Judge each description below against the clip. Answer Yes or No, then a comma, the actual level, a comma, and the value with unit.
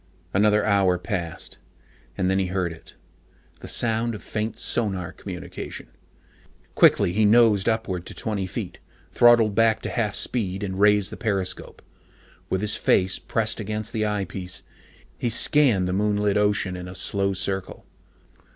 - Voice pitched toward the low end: Yes, low, 105 Hz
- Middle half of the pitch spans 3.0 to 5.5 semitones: No, narrow, 2.5 semitones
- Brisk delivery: No, average, 150 wpm